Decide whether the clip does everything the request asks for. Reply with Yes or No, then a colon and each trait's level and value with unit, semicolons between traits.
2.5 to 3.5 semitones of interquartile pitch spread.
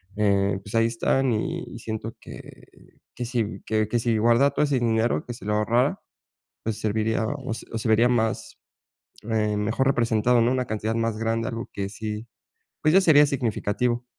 No: narrow, 2.1 semitones